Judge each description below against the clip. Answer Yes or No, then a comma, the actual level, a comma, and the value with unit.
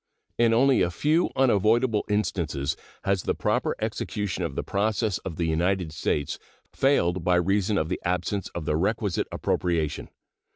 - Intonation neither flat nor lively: Yes, average, 4.0 semitones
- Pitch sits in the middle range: No, very low, 95 Hz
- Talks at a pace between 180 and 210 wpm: No, average, 155 wpm